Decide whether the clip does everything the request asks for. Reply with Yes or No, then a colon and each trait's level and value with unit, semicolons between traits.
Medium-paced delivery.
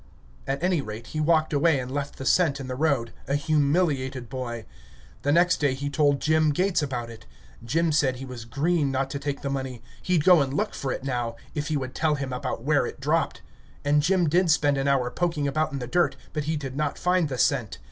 No: fast, 230 wpm